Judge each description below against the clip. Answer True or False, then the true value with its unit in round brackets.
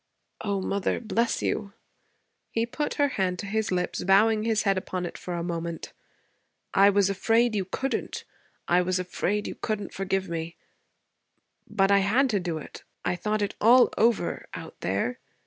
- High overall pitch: True (200 Hz)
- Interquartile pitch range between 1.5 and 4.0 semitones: True (3.3 semitones)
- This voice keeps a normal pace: True (170 wpm)